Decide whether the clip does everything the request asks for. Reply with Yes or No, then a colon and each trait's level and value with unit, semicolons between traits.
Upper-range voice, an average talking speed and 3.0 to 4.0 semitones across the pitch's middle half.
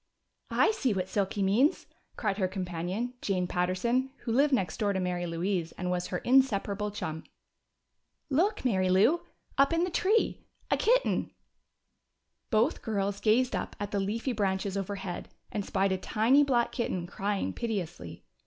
No: high, 200 Hz; average, 155 wpm; average, 4.8 semitones